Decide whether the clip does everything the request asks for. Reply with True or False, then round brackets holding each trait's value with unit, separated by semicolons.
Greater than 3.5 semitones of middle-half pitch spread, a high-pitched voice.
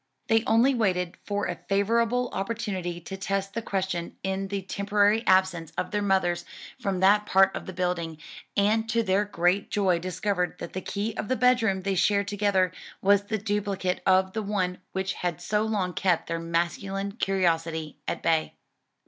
False (2.4 semitones; 195 Hz)